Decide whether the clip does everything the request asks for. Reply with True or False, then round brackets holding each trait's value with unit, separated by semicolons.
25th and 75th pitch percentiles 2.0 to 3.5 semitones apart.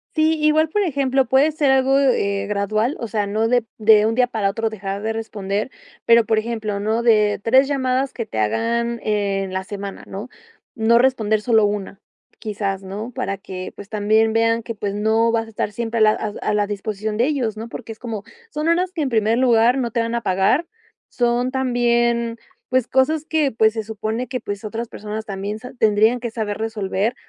True (2.9 semitones)